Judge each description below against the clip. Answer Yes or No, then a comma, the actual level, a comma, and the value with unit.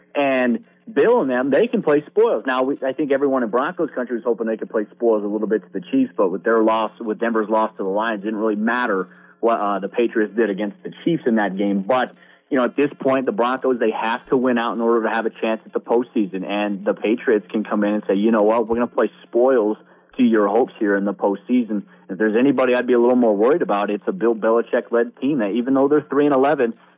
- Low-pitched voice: Yes, low, 115 Hz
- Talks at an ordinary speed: No, fast, 270 wpm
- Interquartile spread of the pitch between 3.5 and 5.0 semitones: No, average, 3.1 semitones